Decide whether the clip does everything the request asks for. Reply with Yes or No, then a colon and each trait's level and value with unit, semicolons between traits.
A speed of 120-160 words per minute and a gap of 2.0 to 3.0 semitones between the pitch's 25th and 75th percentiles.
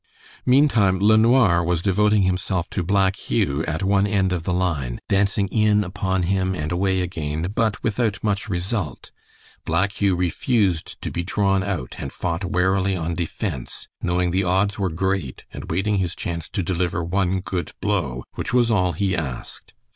No: average, 170 wpm; narrow, 2.6 semitones